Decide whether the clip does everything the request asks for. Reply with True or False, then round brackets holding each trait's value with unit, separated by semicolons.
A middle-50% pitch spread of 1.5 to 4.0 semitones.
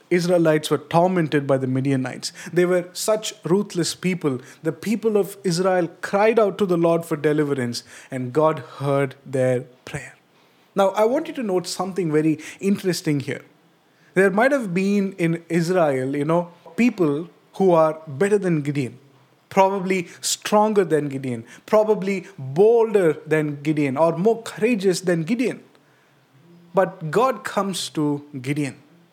False (4.7 semitones)